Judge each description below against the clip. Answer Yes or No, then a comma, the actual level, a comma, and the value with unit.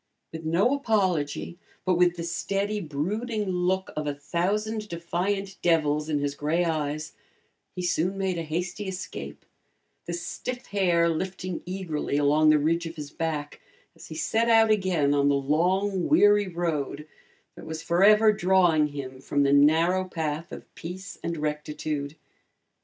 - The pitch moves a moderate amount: Yes, average, 3.9 semitones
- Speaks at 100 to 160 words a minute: Yes, average, 150 wpm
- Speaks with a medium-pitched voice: Yes, medium, 170 Hz